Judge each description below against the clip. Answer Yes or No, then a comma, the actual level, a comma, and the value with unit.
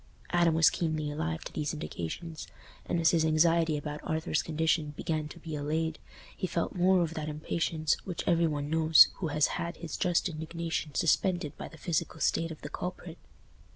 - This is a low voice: No, medium, 160 Hz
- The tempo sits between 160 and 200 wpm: Yes, average, 185 wpm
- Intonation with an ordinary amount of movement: No, narrow, 1.7 semitones